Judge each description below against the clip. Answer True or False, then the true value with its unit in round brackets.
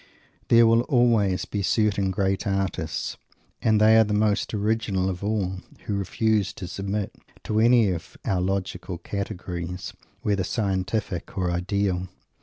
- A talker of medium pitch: False (100 Hz)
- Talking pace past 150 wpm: False (140 wpm)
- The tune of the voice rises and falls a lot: False (2.5 semitones)